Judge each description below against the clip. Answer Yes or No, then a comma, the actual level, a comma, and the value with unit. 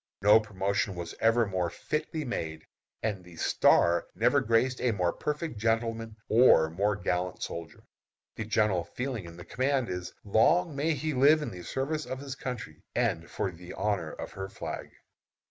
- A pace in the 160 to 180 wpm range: Yes, average, 170 wpm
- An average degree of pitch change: No, wide, 6.3 semitones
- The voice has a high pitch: No, low, 110 Hz